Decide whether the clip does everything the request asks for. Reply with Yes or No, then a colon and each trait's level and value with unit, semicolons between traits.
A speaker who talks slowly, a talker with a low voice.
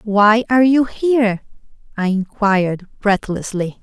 No: slow, 110 wpm; high, 215 Hz